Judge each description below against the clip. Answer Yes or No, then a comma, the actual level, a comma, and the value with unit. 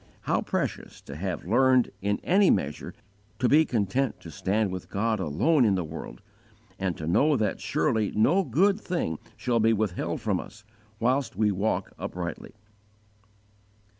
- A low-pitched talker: Yes, low, 110 Hz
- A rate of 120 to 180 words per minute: Yes, average, 160 wpm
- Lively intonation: Yes, wide, 6.0 semitones